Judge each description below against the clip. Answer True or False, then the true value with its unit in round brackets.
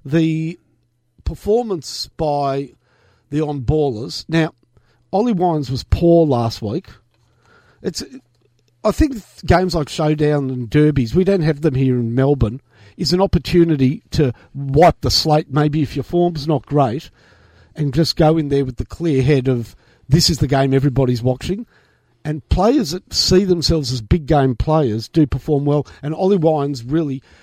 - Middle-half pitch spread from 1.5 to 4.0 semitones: False (4.8 semitones)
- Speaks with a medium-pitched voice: True (145 Hz)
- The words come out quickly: False (155 wpm)